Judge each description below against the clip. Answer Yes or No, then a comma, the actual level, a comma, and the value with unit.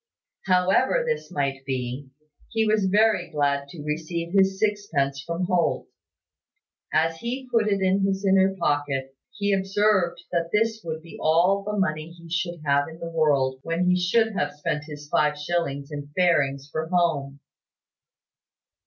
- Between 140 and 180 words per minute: Yes, average, 155 wpm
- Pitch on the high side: No, medium, 170 Hz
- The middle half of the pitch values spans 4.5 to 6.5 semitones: Yes, average, 4.8 semitones